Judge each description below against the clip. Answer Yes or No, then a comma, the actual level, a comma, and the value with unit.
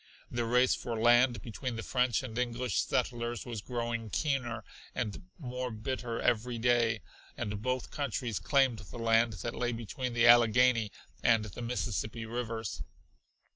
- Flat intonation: Yes, narrow, 1.6 semitones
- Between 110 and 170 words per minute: Yes, average, 145 wpm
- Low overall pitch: Yes, low, 120 Hz